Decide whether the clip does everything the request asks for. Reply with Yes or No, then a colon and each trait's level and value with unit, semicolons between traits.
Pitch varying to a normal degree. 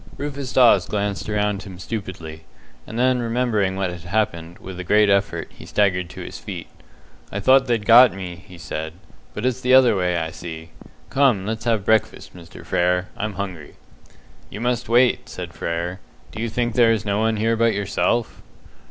Yes: average, 4.4 semitones